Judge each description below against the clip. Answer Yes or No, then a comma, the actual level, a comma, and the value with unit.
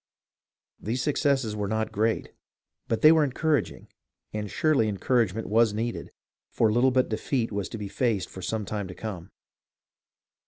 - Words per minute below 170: Yes, average, 155 wpm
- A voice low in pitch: Yes, low, 110 Hz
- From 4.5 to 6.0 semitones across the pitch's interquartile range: No, average, 3.4 semitones